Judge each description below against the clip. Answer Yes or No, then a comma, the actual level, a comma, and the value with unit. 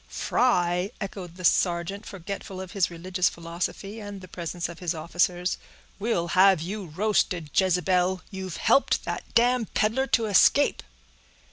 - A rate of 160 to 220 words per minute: No, slow, 135 wpm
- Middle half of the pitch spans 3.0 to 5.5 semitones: No, narrow, 2.5 semitones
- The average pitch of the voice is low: No, medium, 185 Hz